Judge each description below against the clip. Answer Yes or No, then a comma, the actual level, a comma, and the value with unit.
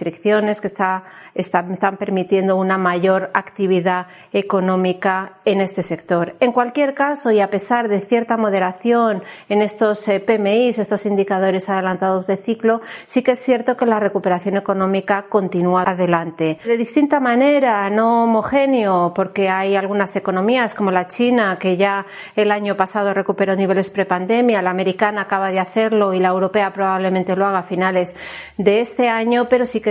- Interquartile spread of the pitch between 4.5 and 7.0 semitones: No, average, 2.8 semitones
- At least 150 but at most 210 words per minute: Yes, average, 155 wpm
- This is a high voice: Yes, high, 200 Hz